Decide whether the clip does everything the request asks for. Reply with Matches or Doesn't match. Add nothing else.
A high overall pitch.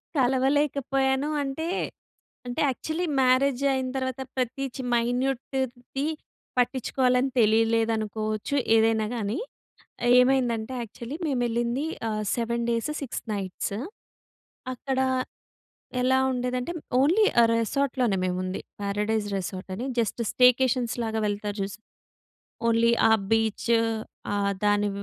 Matches